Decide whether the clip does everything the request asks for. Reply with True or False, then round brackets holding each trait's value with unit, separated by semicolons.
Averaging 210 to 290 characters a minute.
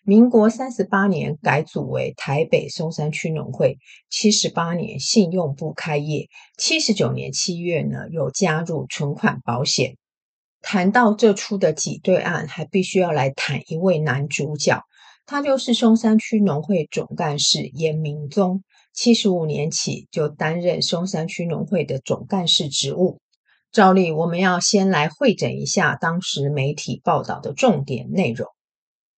True (230 characters per minute)